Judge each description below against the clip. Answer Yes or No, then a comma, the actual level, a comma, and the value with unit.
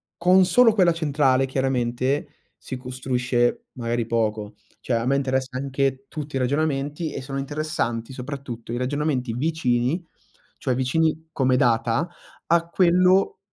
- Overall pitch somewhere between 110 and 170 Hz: Yes, low, 135 Hz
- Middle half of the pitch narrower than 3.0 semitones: No, average, 3.9 semitones